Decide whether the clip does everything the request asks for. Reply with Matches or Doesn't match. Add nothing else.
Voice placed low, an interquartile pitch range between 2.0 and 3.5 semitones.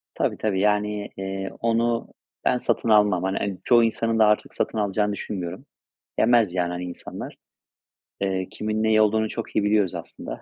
Matches